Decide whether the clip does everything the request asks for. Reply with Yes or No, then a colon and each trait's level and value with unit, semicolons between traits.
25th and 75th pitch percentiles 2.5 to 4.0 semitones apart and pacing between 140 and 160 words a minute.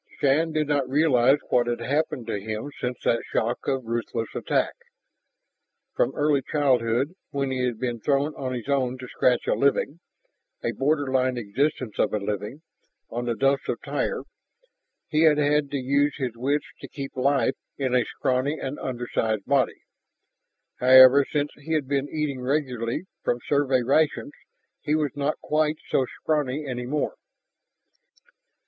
Yes: average, 2.8 semitones; average, 155 wpm